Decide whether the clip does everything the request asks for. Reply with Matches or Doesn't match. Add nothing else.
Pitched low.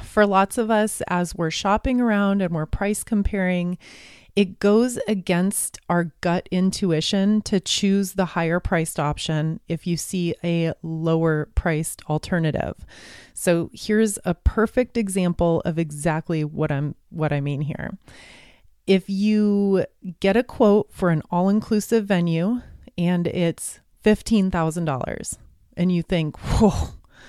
Doesn't match